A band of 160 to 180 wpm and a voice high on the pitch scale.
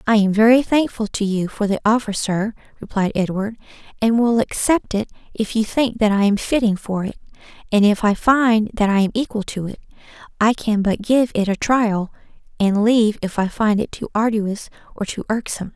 No: average, 200 wpm; high, 215 Hz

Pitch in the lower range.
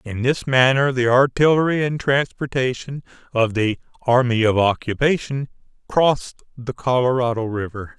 Yes: low, 125 Hz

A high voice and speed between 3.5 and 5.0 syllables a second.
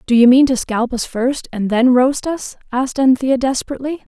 No: very high, 255 Hz; 5.3 syllables/s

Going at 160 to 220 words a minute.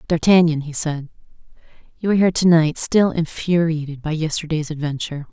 No: average, 145 wpm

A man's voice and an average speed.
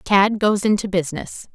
No: female; average, 155 wpm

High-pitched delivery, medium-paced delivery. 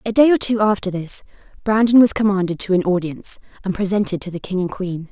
No: high, 200 Hz; fast, 225 wpm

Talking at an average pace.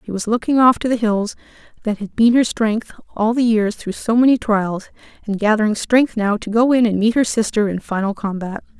No: fast, 225 wpm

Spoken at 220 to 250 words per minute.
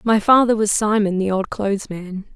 No: fast, 205 wpm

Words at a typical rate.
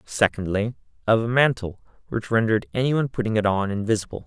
Yes: average, 170 wpm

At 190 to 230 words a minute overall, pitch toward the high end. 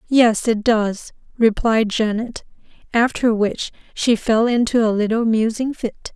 No: slow, 135 wpm; high, 225 Hz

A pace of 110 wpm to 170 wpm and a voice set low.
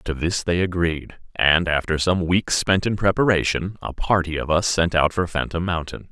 No: average, 195 wpm; very low, 85 Hz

